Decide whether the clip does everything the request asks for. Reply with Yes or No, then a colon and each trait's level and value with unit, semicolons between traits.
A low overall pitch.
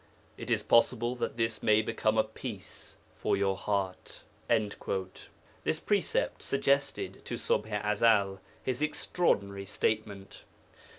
Yes: low, 105 Hz